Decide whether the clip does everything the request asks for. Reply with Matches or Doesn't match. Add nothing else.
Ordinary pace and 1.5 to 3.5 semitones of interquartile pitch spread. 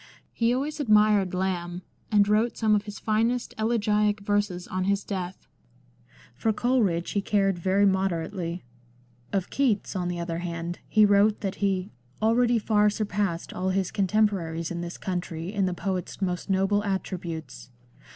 Matches